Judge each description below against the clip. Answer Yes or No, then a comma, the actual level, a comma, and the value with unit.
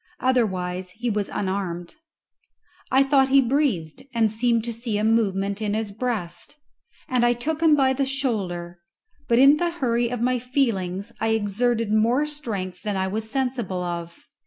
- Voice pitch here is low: No, high, 225 Hz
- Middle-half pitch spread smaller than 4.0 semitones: No, average, 4.6 semitones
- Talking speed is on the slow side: No, average, 165 wpm